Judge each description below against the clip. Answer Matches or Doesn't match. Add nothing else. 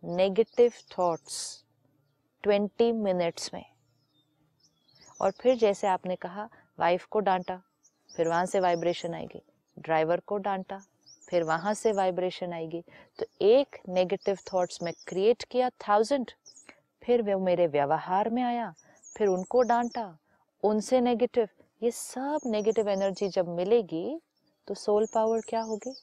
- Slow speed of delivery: Doesn't match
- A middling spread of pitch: Matches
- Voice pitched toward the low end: Doesn't match